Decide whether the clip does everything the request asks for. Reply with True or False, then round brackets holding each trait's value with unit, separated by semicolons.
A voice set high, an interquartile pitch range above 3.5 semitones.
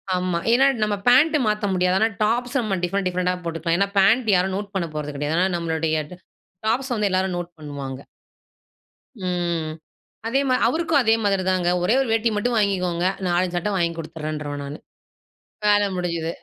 False (180 Hz; 4.1 semitones)